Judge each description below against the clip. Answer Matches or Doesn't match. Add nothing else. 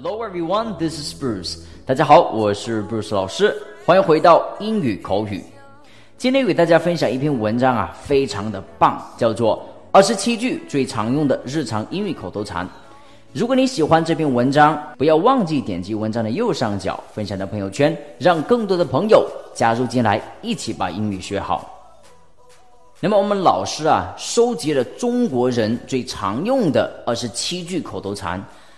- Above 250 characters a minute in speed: Matches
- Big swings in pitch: Matches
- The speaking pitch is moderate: Doesn't match